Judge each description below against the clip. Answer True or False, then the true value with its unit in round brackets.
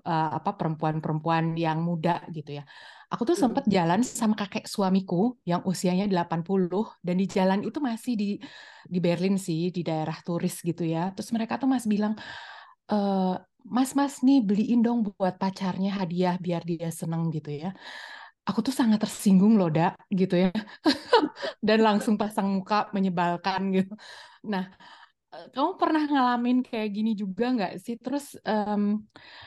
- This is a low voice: False (200 Hz)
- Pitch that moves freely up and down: False (4.9 semitones)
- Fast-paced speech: True (155 wpm)